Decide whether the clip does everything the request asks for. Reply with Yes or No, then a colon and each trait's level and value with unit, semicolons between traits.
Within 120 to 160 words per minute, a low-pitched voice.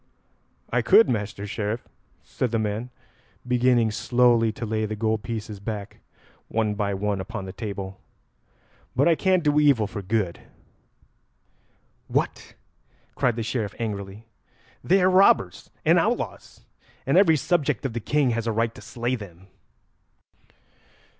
Yes: average, 140 wpm; low, 115 Hz